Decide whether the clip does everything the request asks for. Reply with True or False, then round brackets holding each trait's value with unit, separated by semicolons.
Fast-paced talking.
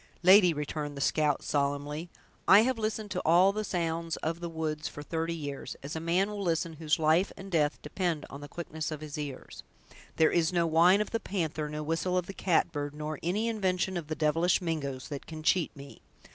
True (210 wpm)